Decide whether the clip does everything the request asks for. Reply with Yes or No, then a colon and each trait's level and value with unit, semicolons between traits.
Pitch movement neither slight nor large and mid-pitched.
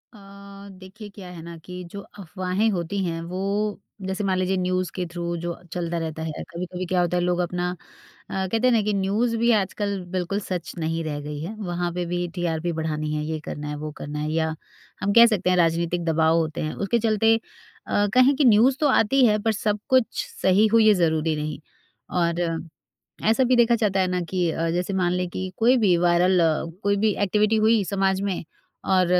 Yes: average, 3.5 semitones; medium, 180 Hz